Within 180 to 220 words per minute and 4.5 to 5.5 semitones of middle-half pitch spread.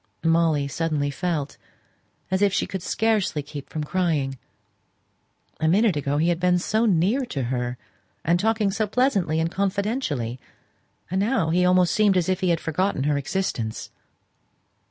No: average, 155 wpm; average, 5.0 semitones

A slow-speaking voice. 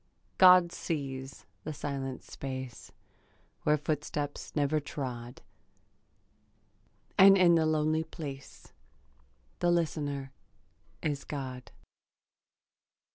Yes: slow, 80 wpm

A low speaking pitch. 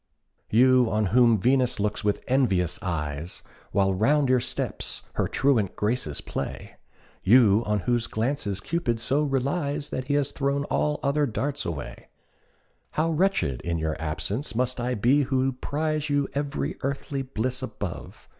Yes: low, 125 Hz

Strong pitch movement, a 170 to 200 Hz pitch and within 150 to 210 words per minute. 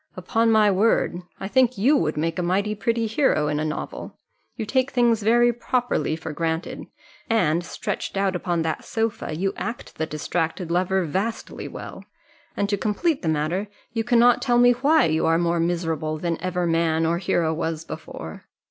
Yes: wide, 5.7 semitones; medium, 185 Hz; average, 180 wpm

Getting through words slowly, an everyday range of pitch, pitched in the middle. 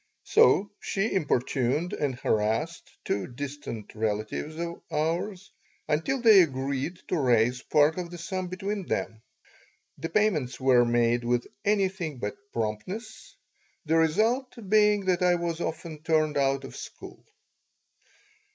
No: slow, 130 wpm; wide, 6.7 semitones; medium, 160 Hz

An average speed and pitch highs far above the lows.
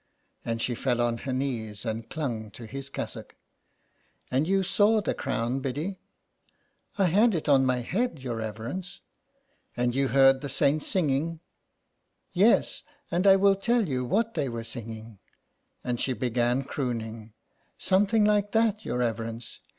Yes: average, 170 wpm; wide, 8.2 semitones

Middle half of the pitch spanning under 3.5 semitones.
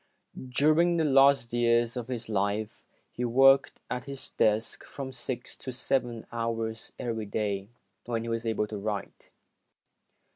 Yes: average, 2.9 semitones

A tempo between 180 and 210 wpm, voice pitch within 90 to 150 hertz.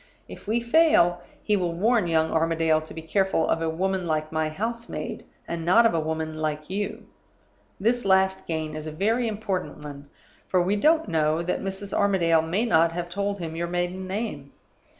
No: average, 190 wpm; medium, 175 Hz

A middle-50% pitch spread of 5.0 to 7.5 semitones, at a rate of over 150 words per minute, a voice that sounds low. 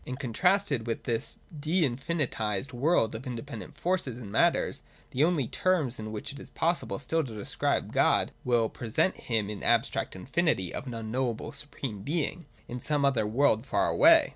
Yes: average, 5.3 semitones; average, 180 wpm; low, 130 Hz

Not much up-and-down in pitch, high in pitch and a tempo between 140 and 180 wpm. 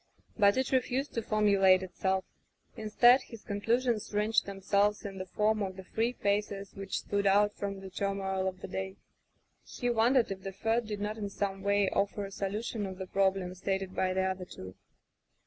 No: narrow, 2.0 semitones; high, 200 Hz; average, 190 wpm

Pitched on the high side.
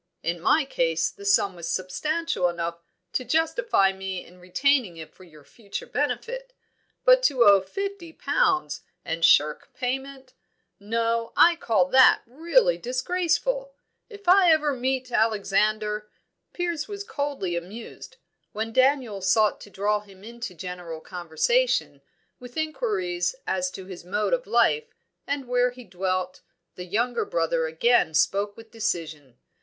Yes: high, 230 Hz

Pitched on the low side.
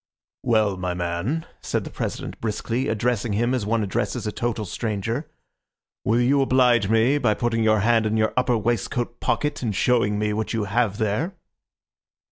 Yes: low, 115 Hz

